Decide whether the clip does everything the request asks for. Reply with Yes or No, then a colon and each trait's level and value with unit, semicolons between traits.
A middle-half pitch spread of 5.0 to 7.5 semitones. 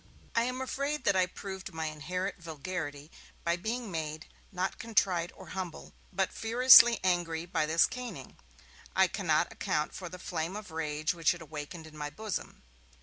No: average, 4.0 semitones